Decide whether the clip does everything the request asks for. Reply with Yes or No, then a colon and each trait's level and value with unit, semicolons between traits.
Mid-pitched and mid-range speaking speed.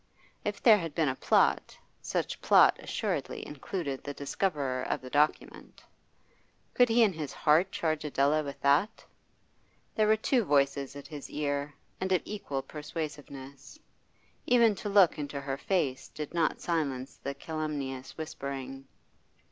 Yes: medium, 150 Hz; average, 145 wpm